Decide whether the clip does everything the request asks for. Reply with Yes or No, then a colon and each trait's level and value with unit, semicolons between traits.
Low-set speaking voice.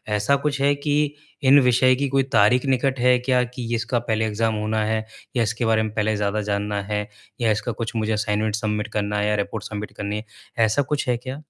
Yes: low, 110 Hz